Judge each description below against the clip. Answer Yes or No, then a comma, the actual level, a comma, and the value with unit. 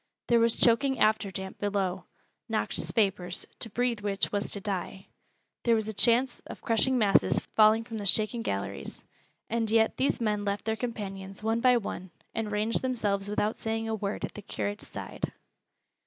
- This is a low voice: No, high, 215 Hz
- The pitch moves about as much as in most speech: No, narrow, 2.3 semitones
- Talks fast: No, average, 175 wpm